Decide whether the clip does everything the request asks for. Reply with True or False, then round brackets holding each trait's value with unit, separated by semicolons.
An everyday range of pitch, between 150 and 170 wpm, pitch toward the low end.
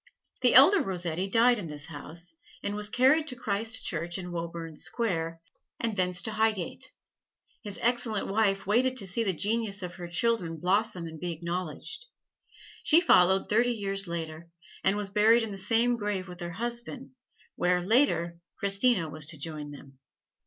False (4.9 semitones; 165 wpm; 195 Hz)